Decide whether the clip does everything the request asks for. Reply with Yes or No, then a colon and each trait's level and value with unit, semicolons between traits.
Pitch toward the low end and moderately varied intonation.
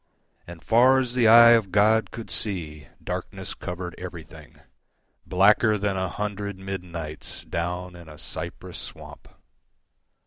Yes: very low, 95 Hz; average, 3.9 semitones